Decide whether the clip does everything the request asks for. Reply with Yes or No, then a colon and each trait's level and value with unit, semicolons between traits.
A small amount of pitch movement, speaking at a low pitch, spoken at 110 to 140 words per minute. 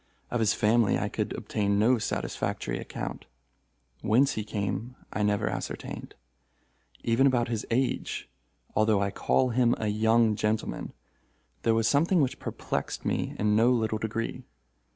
Yes: narrow, 2.3 semitones; low, 110 Hz; slow, 135 wpm